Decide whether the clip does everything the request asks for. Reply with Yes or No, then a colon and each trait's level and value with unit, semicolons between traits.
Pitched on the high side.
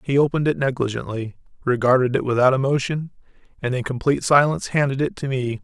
No: low, 135 Hz